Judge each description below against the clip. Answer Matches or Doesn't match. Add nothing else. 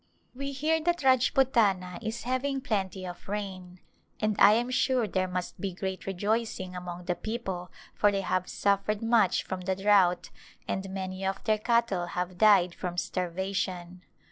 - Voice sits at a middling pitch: Doesn't match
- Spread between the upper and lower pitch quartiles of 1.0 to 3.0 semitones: Doesn't match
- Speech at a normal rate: Matches